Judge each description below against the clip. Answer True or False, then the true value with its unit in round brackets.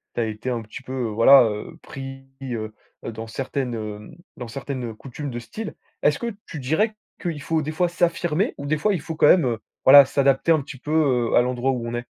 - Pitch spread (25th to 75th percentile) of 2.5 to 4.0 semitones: False (4.4 semitones)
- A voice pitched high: False (135 Hz)